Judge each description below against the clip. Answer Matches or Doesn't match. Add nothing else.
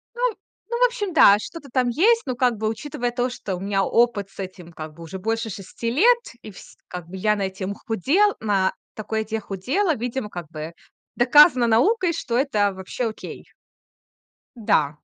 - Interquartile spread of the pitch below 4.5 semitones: Doesn't match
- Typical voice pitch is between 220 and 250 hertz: Matches